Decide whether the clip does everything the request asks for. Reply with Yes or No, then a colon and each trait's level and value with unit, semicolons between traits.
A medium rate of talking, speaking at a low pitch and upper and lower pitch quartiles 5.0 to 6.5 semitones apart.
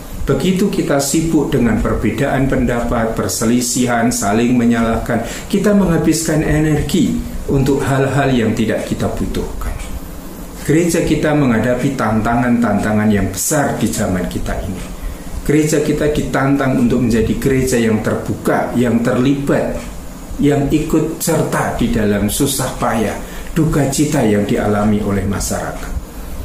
Yes: average, 115 wpm; low, 120 Hz; wide, 5.4 semitones